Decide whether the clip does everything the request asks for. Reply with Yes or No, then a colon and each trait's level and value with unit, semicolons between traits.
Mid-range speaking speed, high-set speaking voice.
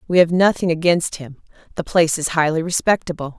No: average, 175 wpm; medium, 165 Hz